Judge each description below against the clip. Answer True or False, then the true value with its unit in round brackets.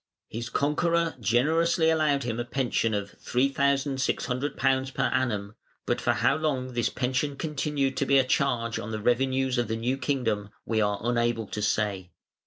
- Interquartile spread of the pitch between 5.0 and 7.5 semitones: False (3.5 semitones)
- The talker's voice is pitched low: True (130 Hz)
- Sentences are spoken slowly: False (165 wpm)